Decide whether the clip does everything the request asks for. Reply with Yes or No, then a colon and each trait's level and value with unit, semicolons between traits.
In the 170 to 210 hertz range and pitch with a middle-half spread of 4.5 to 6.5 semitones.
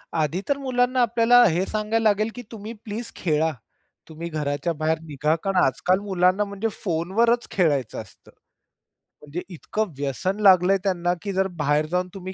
Yes: medium, 185 Hz; average, 5.0 semitones